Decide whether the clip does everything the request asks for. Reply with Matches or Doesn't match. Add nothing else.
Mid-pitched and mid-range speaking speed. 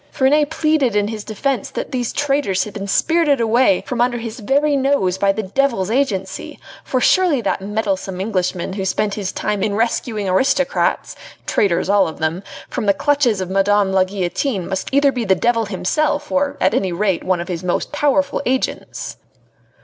Doesn't match